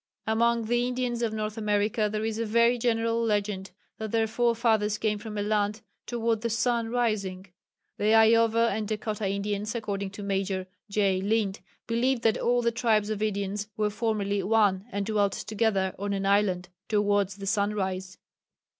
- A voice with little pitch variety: Yes, narrow, 2.2 semitones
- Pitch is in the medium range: No, high, 215 Hz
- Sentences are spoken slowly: No, average, 165 wpm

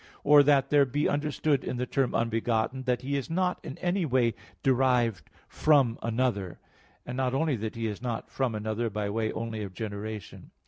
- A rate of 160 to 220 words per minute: Yes, average, 185 wpm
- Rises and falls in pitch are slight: No, average, 3.8 semitones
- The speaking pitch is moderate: No, low, 125 Hz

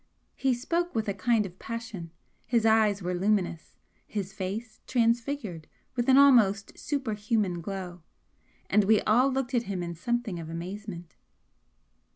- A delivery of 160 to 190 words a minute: No, average, 145 wpm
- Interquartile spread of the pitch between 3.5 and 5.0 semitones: Yes, average, 4.3 semitones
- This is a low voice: No, high, 215 Hz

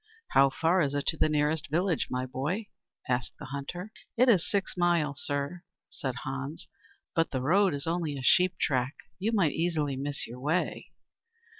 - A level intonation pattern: No, average, 4.3 semitones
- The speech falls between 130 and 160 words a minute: No, average, 175 wpm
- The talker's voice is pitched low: No, medium, 150 Hz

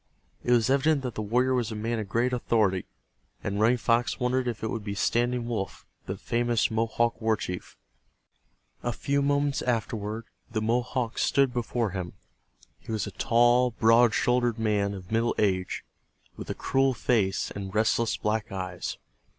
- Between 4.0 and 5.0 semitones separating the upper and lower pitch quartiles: No, narrow, 2.5 semitones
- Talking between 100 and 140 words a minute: No, average, 165 wpm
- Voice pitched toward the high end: No, low, 115 Hz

